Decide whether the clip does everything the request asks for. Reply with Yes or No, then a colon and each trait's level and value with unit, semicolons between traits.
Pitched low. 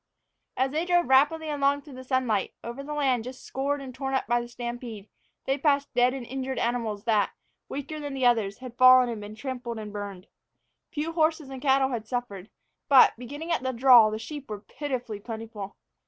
No: very high, 255 Hz